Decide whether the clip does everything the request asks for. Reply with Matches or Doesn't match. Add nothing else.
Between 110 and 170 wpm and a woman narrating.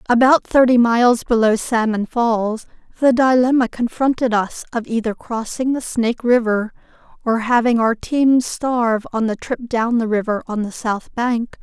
Matches